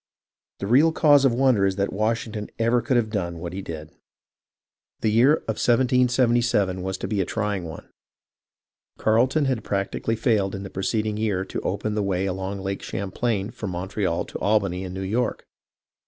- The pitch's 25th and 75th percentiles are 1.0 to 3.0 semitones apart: No, average, 3.6 semitones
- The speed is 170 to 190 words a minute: Yes, average, 175 wpm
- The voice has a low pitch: Yes, low, 105 Hz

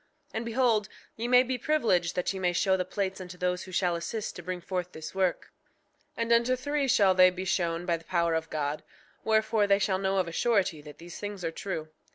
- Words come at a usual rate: No, fast, 235 wpm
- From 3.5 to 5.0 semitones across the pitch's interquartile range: Yes, average, 3.9 semitones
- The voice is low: No, medium, 185 Hz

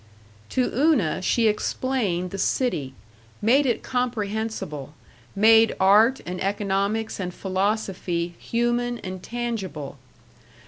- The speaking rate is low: Yes, slow, 100 wpm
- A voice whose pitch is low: No, high, 210 Hz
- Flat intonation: No, average, 4.3 semitones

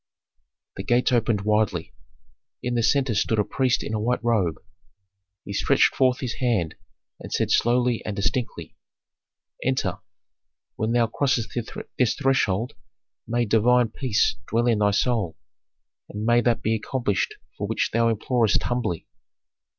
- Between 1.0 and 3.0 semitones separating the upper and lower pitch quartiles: Yes, narrow, 2.6 semitones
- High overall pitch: No, low, 115 Hz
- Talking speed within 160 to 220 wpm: No, average, 145 wpm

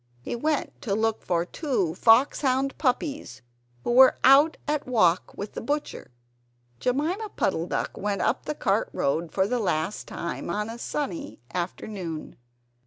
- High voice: Yes, high, 230 Hz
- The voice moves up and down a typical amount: No, wide, 7.0 semitones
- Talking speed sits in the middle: Yes, average, 150 wpm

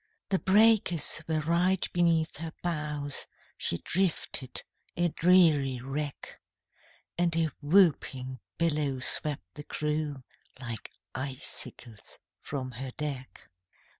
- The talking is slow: Yes, slow, 105 wpm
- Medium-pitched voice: Yes, medium, 150 Hz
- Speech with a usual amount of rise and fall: Yes, average, 4.0 semitones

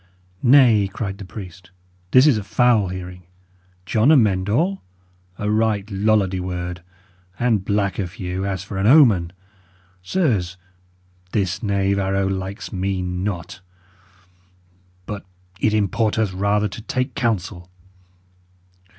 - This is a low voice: Yes, low, 100 Hz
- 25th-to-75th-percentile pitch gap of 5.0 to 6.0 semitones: No, average, 2.9 semitones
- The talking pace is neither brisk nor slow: No, slow, 120 wpm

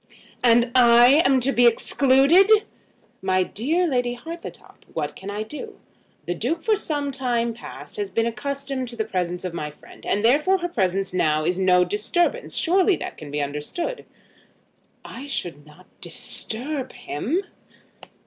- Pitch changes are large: Yes, wide, 7.6 semitones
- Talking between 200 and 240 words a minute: No, average, 155 wpm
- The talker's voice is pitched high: Yes, high, 245 Hz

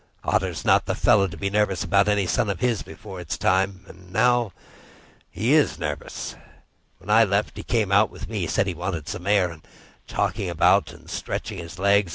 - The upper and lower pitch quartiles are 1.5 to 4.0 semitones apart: Yes, average, 2.7 semitones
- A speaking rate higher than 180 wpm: Yes, average, 190 wpm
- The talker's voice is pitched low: Yes, low, 100 Hz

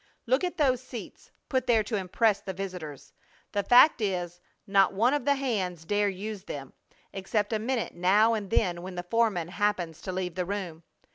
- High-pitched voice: Yes, high, 200 Hz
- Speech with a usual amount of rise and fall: Yes, average, 4.1 semitones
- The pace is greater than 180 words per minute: Yes, average, 190 wpm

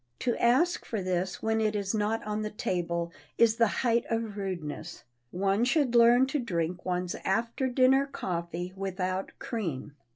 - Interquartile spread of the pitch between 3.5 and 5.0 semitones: Yes, average, 4.5 semitones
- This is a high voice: Yes, high, 210 Hz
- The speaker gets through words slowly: No, average, 160 wpm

